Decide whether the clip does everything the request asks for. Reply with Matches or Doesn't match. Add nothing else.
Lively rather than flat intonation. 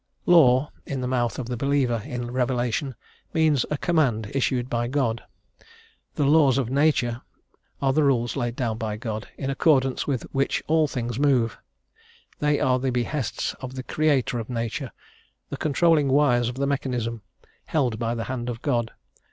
Doesn't match